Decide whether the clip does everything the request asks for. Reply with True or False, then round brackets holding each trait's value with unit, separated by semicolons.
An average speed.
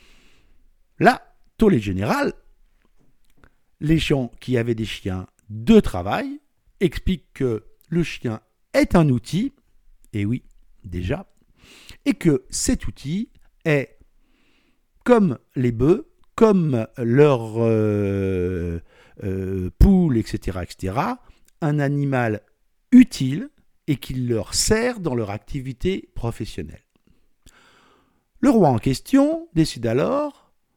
False (105 wpm)